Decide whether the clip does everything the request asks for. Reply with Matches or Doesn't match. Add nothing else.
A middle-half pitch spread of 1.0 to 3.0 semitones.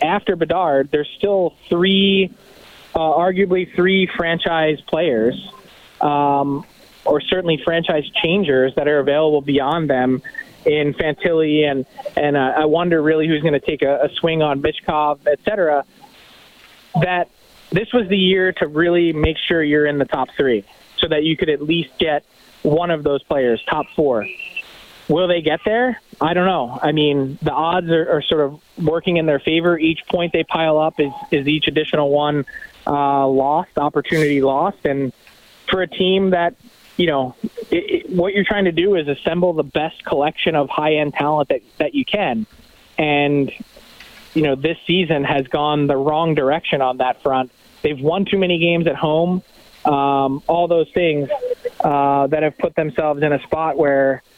Doesn't match